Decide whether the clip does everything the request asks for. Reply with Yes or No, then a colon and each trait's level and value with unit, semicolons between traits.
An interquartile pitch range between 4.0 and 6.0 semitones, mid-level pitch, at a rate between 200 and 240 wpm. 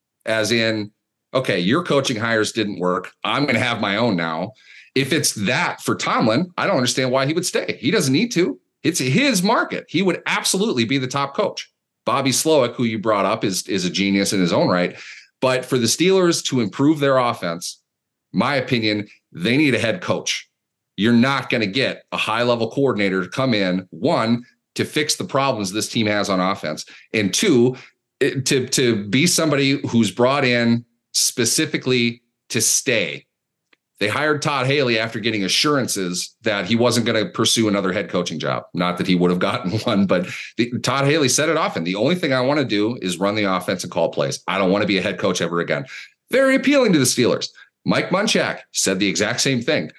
No: average, 4.8 semitones; low, 115 Hz; fast, 205 wpm